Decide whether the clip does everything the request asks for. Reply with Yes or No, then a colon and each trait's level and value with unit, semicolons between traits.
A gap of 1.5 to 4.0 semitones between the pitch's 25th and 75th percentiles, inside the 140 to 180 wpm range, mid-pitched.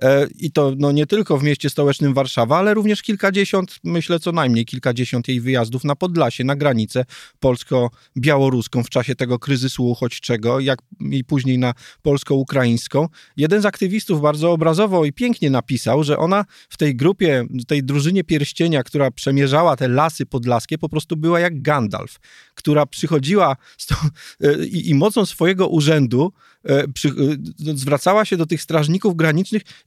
No: average, 4.4 semitones; average, 155 wpm; medium, 145 Hz